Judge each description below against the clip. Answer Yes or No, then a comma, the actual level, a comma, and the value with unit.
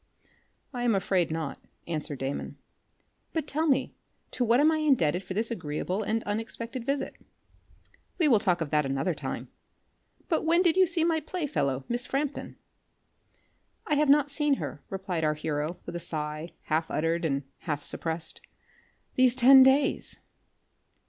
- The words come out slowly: No, average, 160 wpm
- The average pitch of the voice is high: Yes, high, 215 Hz